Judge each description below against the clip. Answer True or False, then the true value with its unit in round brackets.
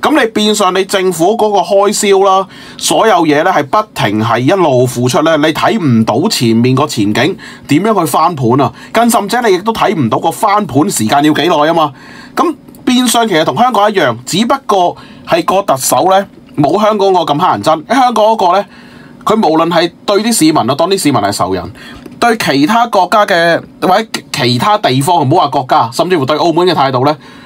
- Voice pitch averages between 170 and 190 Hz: True (185 Hz)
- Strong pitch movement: True (6.6 semitones)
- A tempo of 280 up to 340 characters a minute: True (295 characters per minute)